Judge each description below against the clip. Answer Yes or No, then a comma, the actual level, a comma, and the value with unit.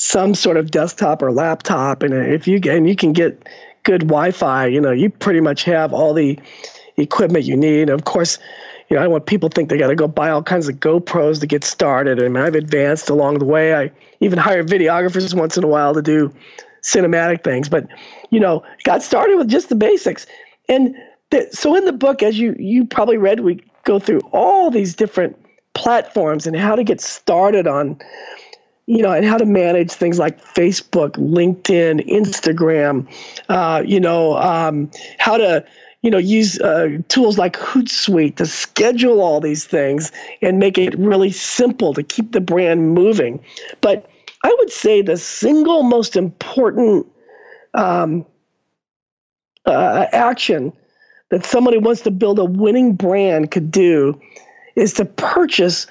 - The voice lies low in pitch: No, medium, 180 Hz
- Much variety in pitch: Yes, wide, 6.4 semitones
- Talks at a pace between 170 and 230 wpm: Yes, average, 175 wpm